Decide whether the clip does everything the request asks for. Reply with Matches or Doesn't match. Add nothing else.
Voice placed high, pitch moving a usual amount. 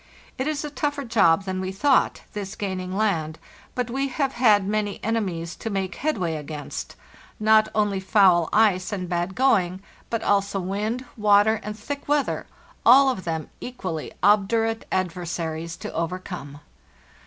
Matches